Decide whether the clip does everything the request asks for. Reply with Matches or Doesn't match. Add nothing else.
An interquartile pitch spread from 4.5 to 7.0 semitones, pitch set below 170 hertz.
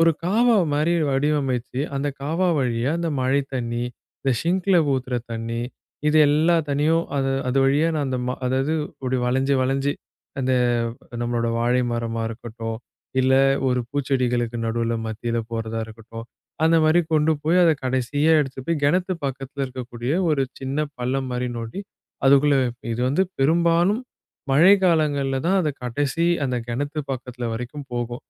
Doesn't match